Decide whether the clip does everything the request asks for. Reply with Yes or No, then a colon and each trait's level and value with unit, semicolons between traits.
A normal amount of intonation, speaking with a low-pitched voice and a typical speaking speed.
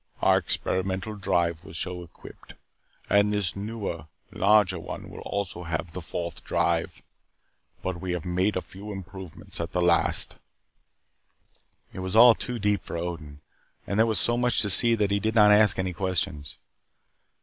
Yes: average, 3.0 semitones; very low, 95 Hz; average, 165 wpm